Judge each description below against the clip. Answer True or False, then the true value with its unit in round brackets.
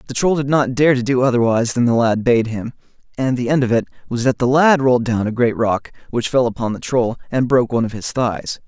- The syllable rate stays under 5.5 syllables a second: False (6.0 syllables/s)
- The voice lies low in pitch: True (125 Hz)